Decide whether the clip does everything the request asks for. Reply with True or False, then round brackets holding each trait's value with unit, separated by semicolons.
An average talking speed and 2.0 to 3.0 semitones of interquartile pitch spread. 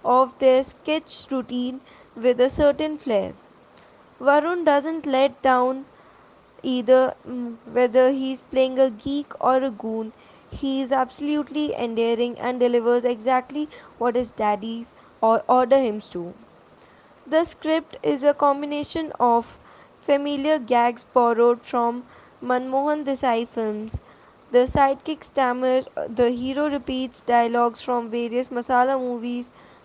False (120 wpm; 2.6 semitones)